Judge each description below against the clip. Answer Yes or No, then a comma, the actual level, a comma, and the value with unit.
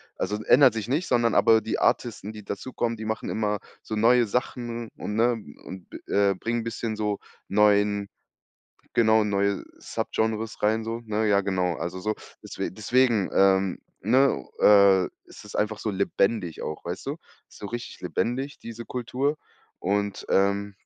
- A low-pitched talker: Yes, low, 110 Hz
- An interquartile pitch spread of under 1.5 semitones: No, narrow, 2.6 semitones